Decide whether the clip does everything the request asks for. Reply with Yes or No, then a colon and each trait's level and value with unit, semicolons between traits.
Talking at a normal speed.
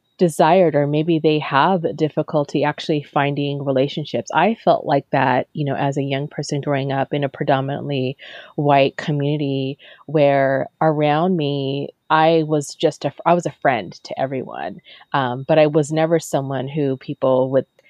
Yes: average, 160 wpm